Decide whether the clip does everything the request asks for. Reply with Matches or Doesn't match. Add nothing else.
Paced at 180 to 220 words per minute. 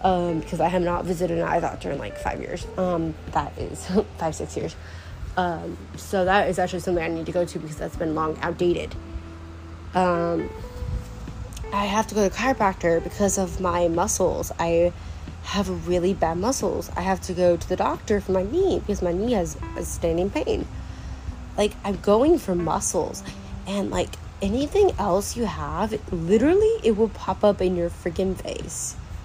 Matches